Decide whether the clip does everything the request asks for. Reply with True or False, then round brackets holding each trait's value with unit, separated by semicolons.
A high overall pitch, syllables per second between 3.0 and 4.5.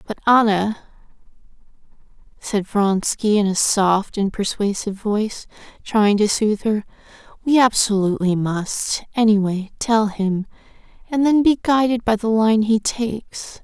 True (215 Hz; 4.3 syllables/s)